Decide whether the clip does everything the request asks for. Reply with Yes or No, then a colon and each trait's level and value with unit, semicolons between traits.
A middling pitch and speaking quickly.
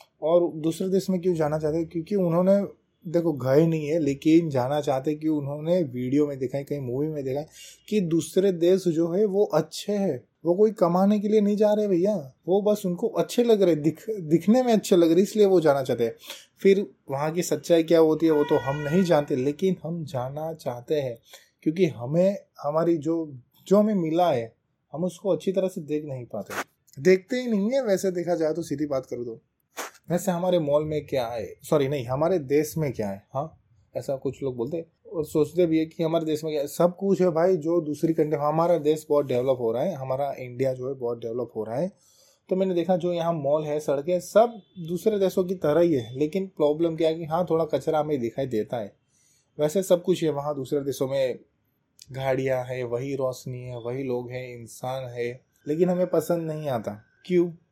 Yes: medium, 160 Hz; fast, 220 wpm